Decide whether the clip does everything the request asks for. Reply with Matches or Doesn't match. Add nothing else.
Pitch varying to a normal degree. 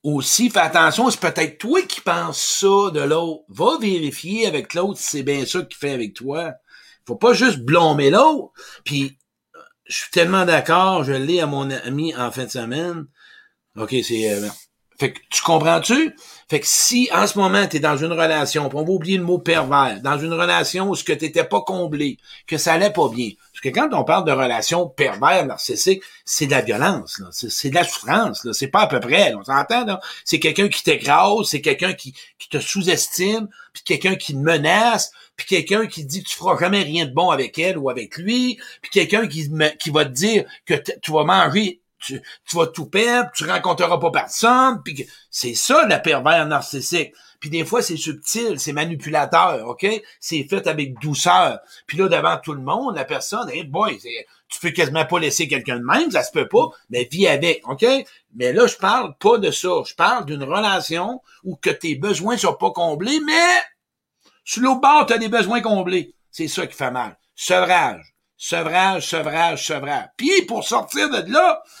Doesn't match